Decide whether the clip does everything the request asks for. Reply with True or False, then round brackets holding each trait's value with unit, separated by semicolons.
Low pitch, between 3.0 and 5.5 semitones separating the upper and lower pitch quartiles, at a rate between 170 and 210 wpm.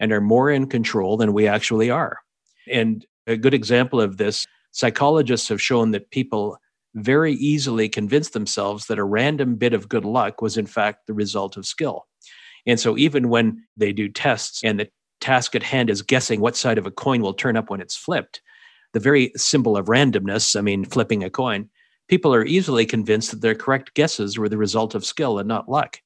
True (115 Hz; 4.1 semitones; 205 wpm)